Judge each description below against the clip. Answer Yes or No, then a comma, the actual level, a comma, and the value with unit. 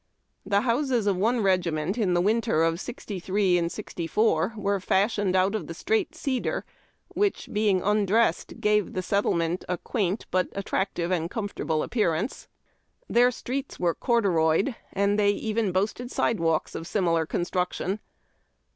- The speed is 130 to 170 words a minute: Yes, average, 140 wpm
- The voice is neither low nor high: No, high, 200 Hz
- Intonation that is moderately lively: Yes, average, 3.9 semitones